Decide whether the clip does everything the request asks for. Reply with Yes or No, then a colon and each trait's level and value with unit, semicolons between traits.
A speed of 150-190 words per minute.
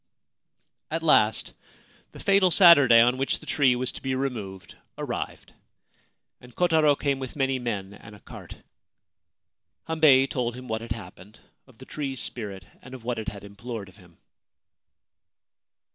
Yes: average, 160 wpm